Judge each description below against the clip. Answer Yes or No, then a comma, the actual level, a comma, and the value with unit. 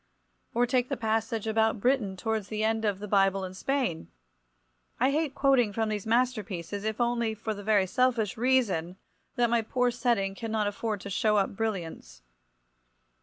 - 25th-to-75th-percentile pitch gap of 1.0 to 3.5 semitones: Yes, average, 3.1 semitones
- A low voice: No, high, 220 Hz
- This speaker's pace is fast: No, average, 170 wpm